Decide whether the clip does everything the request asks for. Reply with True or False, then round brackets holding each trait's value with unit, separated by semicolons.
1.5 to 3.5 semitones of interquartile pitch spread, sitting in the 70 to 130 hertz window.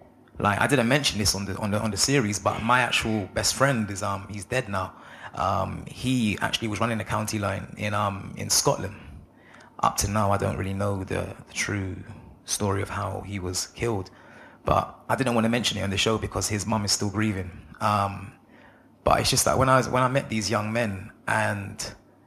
True (2.6 semitones; 105 Hz)